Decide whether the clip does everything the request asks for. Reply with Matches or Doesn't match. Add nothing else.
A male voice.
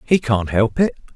Matches